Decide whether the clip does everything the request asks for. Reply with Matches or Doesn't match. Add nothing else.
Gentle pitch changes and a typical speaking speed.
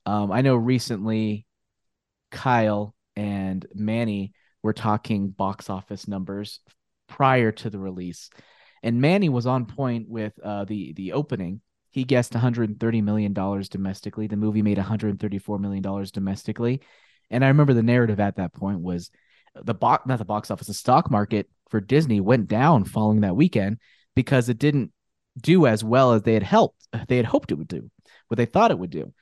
Doesn't match